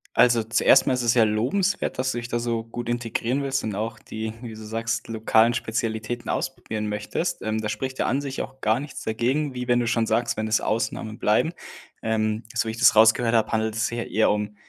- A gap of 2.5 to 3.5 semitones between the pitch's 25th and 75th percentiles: No, narrow, 1.8 semitones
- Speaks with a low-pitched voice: Yes, low, 115 Hz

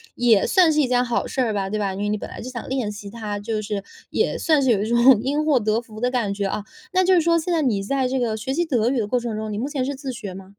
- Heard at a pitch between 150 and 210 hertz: No, high, 235 Hz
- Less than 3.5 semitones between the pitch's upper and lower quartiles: No, average, 4.1 semitones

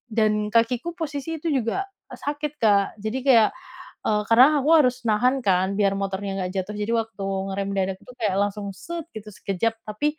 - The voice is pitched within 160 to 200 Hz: No, high, 220 Hz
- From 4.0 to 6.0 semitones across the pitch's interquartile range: Yes, average, 4.3 semitones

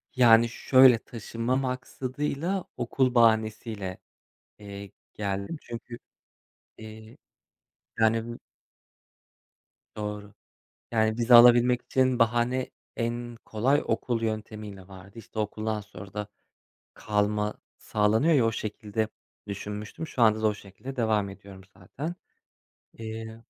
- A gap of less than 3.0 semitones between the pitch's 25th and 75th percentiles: Yes, narrow, 2.5 semitones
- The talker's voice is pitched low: Yes, low, 110 Hz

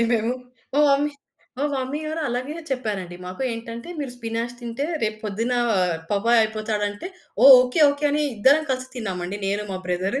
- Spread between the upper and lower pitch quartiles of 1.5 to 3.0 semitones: No, average, 4.4 semitones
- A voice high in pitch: Yes, high, 235 Hz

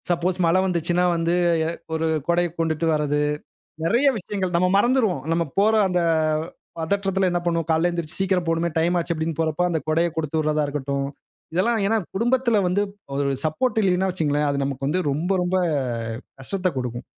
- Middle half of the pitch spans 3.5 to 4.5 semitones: No, average, 3.1 semitones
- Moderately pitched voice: Yes, medium, 170 Hz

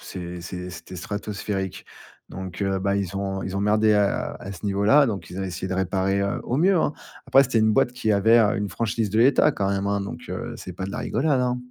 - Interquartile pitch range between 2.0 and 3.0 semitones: Yes, narrow, 2.5 semitones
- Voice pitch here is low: Yes, low, 100 Hz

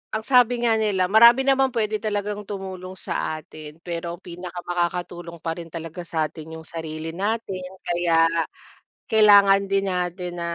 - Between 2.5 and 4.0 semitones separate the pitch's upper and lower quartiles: Yes, average, 3.7 semitones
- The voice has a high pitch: No, medium, 180 Hz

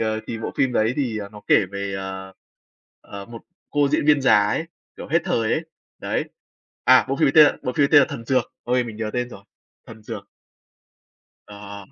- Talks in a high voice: No, low, 115 Hz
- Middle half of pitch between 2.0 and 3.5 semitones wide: No, average, 4.5 semitones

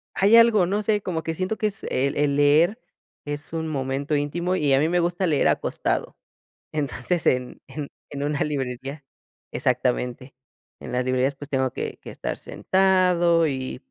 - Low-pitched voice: No, medium, 150 Hz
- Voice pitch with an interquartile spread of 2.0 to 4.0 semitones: No, average, 4.7 semitones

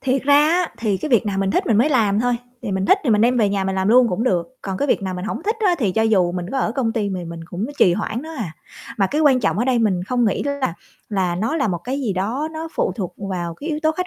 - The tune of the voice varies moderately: No, wide, 5.9 semitones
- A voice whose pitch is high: Yes, high, 220 Hz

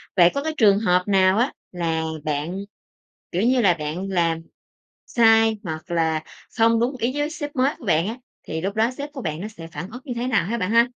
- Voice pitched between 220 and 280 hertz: No, high, 200 Hz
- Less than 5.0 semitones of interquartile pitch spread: No, wide, 5.6 semitones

